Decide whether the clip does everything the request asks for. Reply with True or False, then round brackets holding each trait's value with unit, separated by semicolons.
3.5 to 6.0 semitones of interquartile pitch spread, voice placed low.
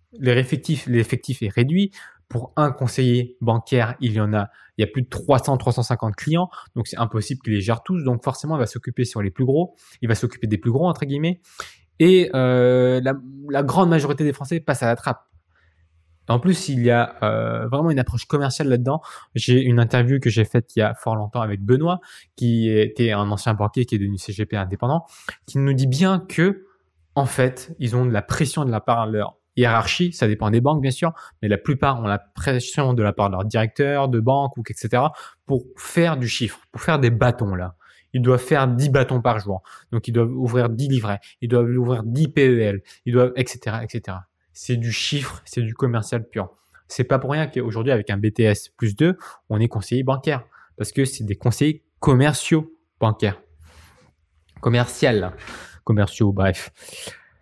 True (3.9 semitones; 125 Hz)